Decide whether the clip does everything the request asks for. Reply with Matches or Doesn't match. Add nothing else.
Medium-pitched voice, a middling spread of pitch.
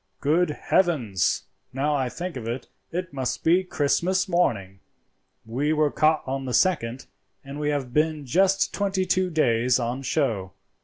Doesn't match